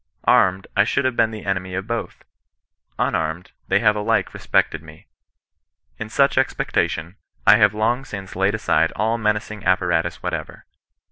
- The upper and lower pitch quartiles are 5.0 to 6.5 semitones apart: No, average, 2.9 semitones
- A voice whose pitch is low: Yes, low, 105 Hz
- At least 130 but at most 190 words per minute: Yes, average, 150 wpm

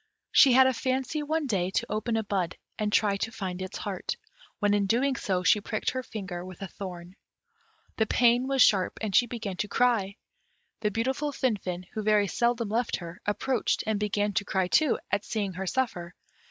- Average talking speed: Yes, average, 195 wpm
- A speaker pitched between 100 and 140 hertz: No, high, 210 Hz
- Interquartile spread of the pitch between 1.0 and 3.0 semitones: No, average, 4.2 semitones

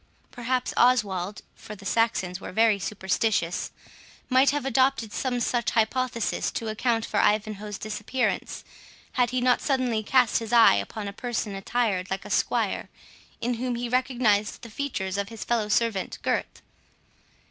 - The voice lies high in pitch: Yes, high, 230 Hz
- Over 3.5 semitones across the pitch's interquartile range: No, average, 3.2 semitones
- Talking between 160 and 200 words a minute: No, average, 150 wpm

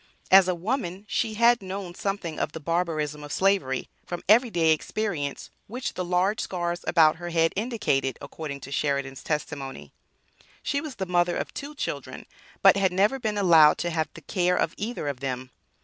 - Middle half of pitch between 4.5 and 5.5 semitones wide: Yes, average, 4.8 semitones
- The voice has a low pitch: No, medium, 175 Hz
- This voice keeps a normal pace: Yes, average, 180 wpm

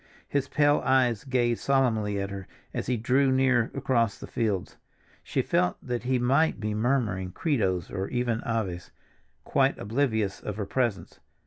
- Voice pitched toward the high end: No, low, 120 Hz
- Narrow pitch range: No, average, 4.2 semitones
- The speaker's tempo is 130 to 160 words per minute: Yes, average, 155 wpm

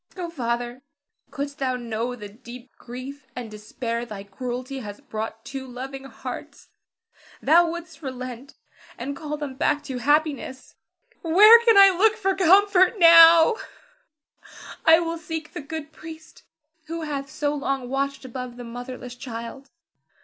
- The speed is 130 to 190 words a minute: Yes, average, 145 wpm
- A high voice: Yes, very high, 275 Hz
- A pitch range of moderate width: Yes, average, 4.8 semitones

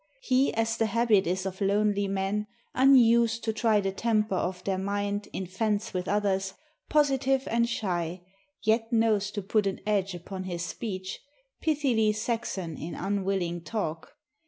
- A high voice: Yes, high, 205 Hz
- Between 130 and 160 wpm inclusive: Yes, average, 155 wpm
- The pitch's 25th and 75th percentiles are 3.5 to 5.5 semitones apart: No, average, 3.1 semitones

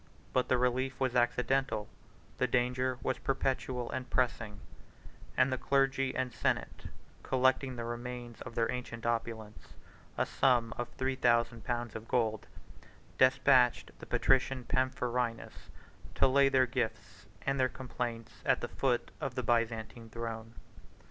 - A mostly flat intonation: Yes, narrow, 1.9 semitones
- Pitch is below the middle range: Yes, low, 125 Hz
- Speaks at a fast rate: No, average, 140 wpm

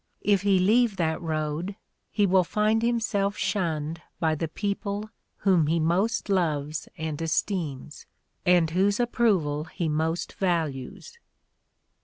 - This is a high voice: No, medium, 175 Hz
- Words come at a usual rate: No, slow, 125 wpm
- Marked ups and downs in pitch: No, average, 4.3 semitones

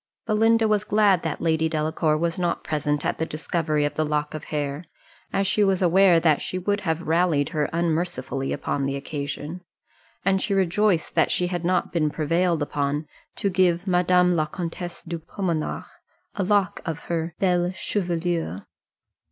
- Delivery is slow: No, average, 170 wpm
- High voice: No, medium, 170 Hz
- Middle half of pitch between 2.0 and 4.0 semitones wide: Yes, average, 3.1 semitones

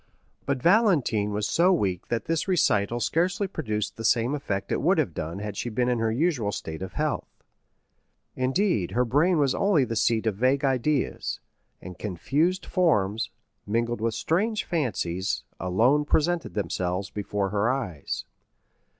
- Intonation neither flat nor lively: No, wide, 7.1 semitones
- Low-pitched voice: Yes, low, 120 Hz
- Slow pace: No, average, 155 wpm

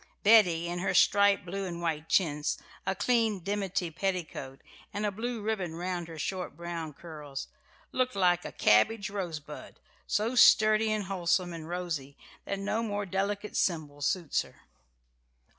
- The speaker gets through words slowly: No, average, 150 wpm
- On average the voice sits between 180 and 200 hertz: Yes, medium, 185 Hz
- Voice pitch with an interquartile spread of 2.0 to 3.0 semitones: No, average, 3.6 semitones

